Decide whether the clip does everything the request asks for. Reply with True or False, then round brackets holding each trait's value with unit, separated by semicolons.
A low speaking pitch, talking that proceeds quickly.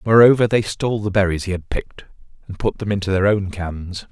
True (100 Hz; 220 wpm)